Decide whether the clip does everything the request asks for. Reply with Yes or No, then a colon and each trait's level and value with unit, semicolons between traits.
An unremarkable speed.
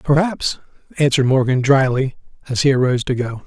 Yes: average, 155 wpm